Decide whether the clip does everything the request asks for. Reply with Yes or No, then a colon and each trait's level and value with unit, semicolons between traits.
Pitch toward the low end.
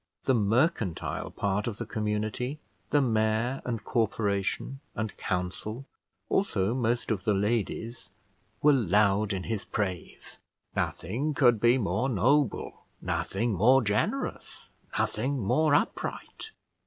Yes: low, 110 Hz